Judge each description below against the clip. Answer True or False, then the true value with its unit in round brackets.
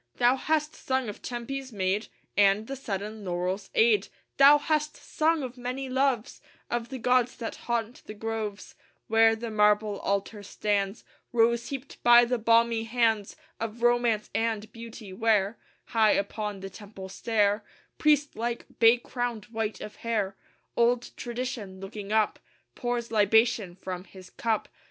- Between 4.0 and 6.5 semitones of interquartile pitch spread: False (2.7 semitones)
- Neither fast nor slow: True (145 wpm)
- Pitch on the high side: True (225 Hz)